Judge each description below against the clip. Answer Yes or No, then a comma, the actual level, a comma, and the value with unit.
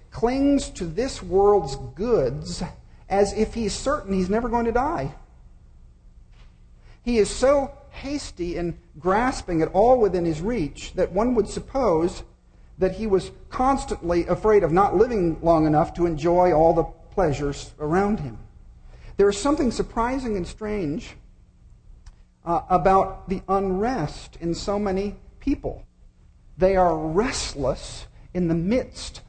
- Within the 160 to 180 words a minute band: No, slow, 135 wpm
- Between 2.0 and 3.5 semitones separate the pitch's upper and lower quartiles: No, average, 5.1 semitones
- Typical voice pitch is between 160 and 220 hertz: Yes, high, 190 Hz